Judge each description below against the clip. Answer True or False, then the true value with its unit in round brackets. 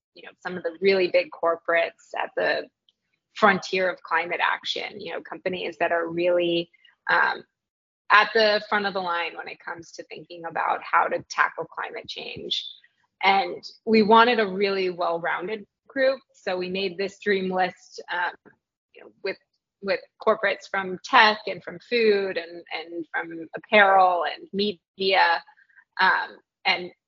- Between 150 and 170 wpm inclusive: True (155 wpm)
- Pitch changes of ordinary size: True (3.4 semitones)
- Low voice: False (190 Hz)